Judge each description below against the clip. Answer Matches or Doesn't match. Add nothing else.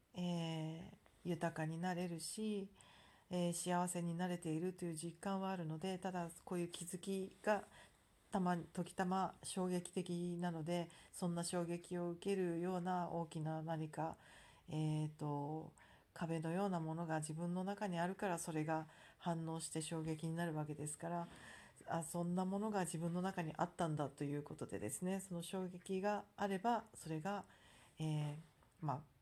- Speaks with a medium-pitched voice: Matches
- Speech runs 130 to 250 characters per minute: Doesn't match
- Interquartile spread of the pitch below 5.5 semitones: Matches